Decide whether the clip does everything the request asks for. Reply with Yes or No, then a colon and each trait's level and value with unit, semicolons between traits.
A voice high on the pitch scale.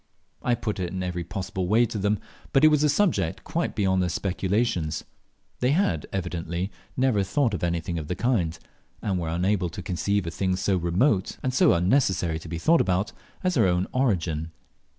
No: very low, 95 Hz